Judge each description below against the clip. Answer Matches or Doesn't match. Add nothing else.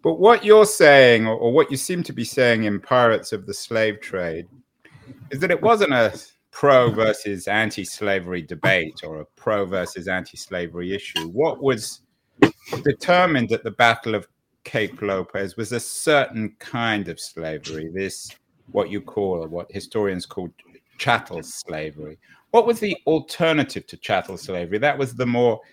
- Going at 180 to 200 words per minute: Doesn't match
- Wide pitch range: Matches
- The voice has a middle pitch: Doesn't match